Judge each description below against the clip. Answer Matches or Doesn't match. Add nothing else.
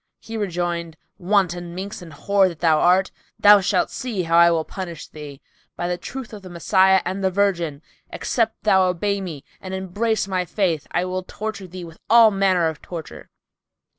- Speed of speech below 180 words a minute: Doesn't match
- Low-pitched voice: Doesn't match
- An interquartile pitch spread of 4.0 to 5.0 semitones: Doesn't match